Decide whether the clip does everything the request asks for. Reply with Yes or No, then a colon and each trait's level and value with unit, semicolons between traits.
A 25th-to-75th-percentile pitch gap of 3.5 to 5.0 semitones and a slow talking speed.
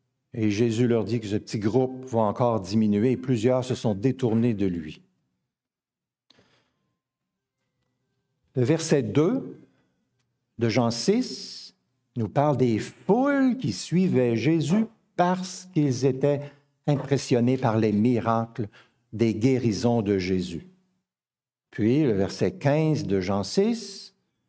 Yes: average, 4.4 semitones; slow, 120 wpm